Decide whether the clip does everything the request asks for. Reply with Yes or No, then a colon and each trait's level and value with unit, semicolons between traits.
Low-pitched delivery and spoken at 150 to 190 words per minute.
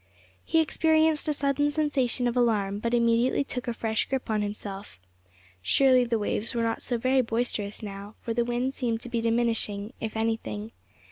No: high, 235 Hz; average, 180 wpm